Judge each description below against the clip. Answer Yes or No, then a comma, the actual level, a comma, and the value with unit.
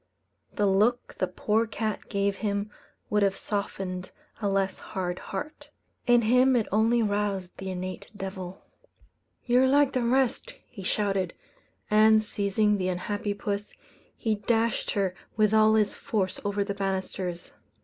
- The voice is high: Yes, high, 205 Hz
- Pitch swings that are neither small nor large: No, narrow, 2.3 semitones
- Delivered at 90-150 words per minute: Yes, average, 145 wpm